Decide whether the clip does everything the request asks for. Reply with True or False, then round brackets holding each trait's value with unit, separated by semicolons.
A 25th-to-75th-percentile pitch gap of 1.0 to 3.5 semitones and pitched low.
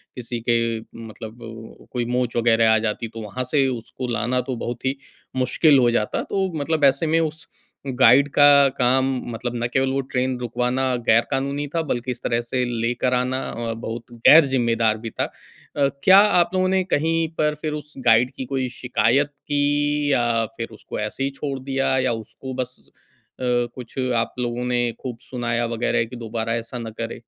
True (2.9 semitones; 125 Hz)